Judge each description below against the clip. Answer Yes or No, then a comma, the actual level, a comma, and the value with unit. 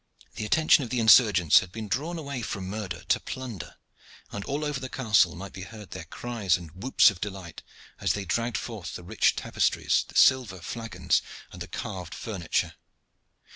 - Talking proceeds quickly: No, average, 180 wpm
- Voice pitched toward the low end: Yes, low, 105 Hz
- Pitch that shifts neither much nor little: Yes, average, 4.7 semitones